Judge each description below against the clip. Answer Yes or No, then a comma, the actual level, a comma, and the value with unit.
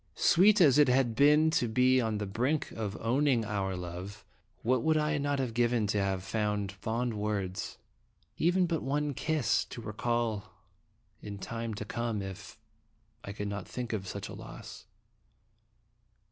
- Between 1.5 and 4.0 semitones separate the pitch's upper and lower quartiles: No, average, 4.8 semitones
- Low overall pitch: Yes, low, 115 Hz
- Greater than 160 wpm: Yes, average, 170 wpm